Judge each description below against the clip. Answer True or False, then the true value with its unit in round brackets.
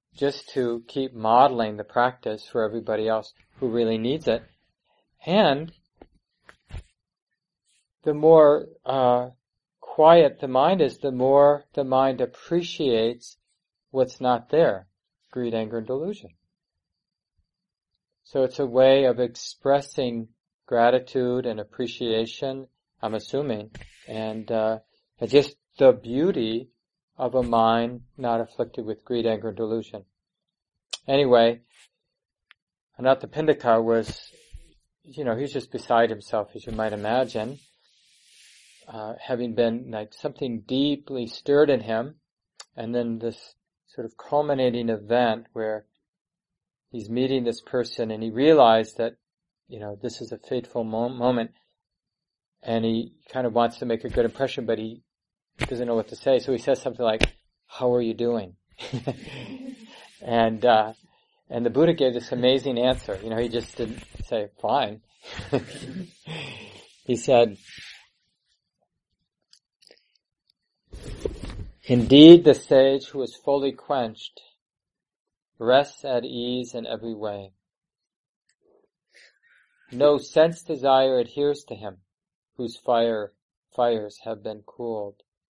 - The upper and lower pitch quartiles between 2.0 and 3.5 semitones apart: True (2.8 semitones)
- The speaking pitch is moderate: False (120 Hz)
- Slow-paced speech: True (120 wpm)